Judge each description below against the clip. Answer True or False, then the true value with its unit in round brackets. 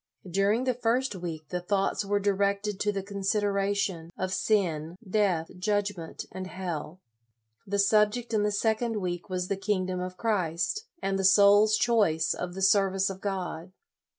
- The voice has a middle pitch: False (195 Hz)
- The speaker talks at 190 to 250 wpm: False (155 wpm)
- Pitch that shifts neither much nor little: False (2.3 semitones)